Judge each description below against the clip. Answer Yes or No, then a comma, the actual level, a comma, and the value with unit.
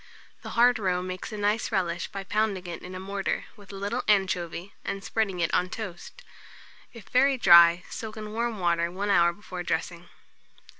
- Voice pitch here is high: Yes, high, 195 Hz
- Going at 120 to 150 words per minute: No, average, 185 wpm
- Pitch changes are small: No, average, 3.3 semitones